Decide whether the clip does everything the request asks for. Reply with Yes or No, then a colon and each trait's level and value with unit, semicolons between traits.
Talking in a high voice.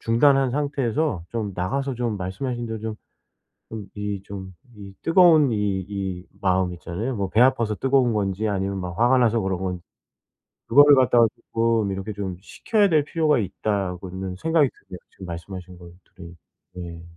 No: low, 105 Hz